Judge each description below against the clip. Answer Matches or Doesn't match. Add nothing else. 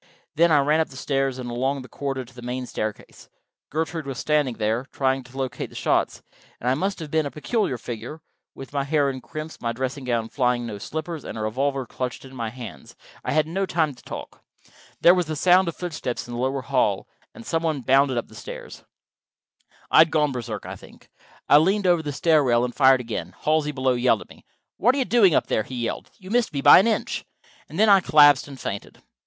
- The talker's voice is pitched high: Doesn't match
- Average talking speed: Doesn't match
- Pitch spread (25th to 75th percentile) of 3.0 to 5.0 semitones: Matches